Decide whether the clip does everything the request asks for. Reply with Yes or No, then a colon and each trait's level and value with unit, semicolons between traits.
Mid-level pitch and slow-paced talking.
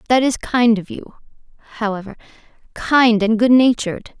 No: high, 230 Hz; slow, 115 wpm